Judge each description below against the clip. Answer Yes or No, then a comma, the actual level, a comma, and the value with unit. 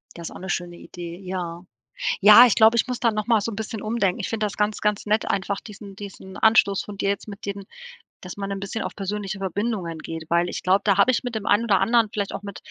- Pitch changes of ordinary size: No, narrow, 2.3 semitones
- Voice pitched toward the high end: Yes, high, 200 Hz